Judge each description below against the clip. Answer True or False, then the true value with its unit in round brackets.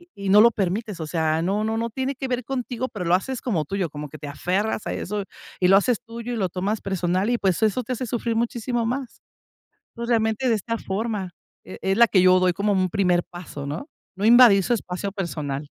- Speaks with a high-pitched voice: True (205 Hz)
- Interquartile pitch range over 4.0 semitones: True (4.4 semitones)